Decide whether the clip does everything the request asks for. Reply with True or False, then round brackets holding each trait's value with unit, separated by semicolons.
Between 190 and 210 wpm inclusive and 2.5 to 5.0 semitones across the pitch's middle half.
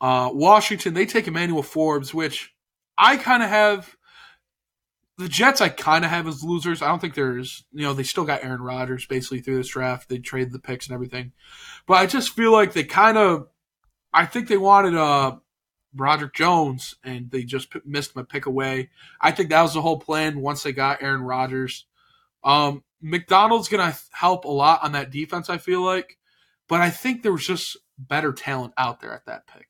False (200 wpm; 5.6 semitones)